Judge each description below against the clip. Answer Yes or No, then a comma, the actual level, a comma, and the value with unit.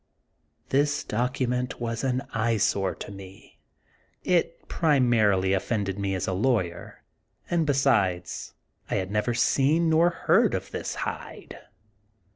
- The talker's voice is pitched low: Yes, low, 115 Hz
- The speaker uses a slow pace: Yes, slow, 125 wpm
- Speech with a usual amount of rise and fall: No, wide, 5.8 semitones